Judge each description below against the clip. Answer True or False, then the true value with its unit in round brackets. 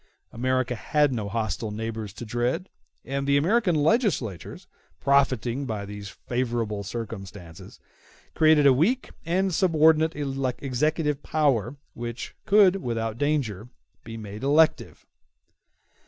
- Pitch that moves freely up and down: True (5.7 semitones)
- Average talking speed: False (110 wpm)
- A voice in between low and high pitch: False (130 Hz)